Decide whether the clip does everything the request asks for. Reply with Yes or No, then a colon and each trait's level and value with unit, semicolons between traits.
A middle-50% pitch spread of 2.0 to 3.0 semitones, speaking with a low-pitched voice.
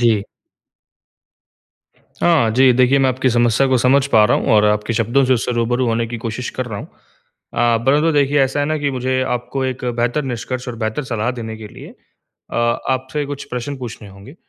Yes: narrow, 2.6 semitones; low, 125 Hz